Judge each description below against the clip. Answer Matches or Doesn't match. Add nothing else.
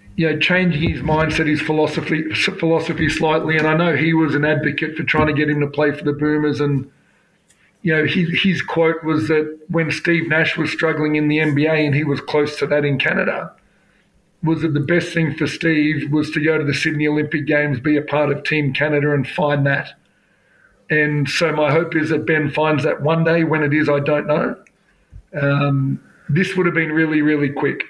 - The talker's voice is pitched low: Doesn't match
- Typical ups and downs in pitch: Doesn't match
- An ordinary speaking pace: Doesn't match